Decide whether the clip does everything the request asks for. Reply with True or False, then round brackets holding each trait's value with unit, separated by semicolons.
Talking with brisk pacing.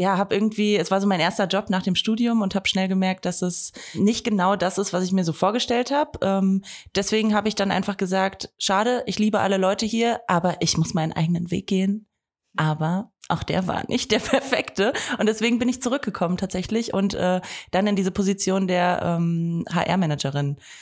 True (200 wpm)